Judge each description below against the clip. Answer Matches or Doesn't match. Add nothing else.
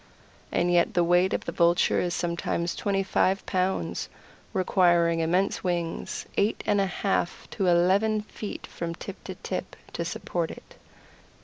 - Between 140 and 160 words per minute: Matches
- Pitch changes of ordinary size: Doesn't match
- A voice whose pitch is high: Doesn't match